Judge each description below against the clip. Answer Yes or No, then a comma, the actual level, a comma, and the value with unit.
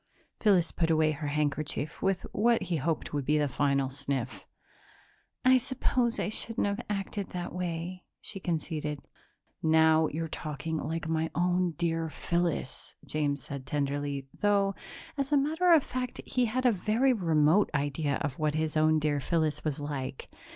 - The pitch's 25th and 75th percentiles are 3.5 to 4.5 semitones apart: No, average, 5.0 semitones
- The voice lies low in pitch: No, medium, 160 Hz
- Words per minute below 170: Yes, average, 160 wpm